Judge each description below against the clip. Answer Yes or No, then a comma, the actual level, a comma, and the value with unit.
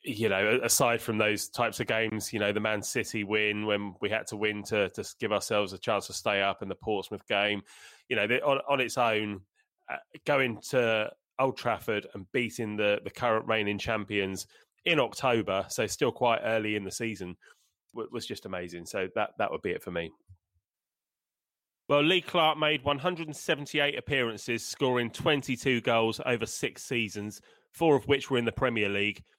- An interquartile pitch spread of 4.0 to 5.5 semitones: Yes, average, 4.4 semitones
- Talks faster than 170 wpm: Yes, average, 190 wpm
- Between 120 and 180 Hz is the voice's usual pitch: No, low, 110 Hz